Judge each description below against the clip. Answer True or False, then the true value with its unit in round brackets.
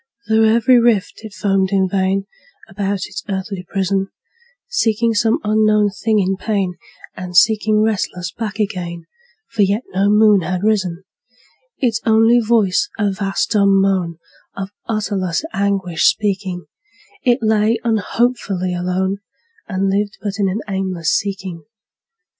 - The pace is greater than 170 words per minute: False (135 wpm)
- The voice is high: True (200 Hz)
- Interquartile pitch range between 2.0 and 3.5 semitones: True (2.5 semitones)